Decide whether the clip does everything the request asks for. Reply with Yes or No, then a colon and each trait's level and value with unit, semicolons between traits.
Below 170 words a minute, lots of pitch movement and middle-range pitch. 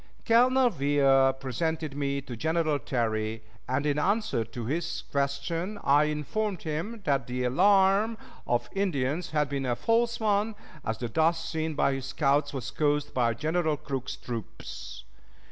No: average, 150 wpm; average, 4.8 semitones; medium, 150 Hz